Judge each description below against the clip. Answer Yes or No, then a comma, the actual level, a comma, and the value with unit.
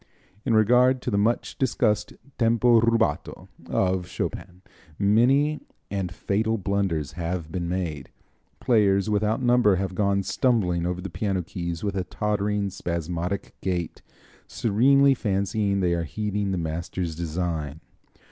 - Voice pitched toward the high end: No, low, 100 Hz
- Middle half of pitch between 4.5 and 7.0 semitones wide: No, average, 3.8 semitones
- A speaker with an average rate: No, slow, 130 wpm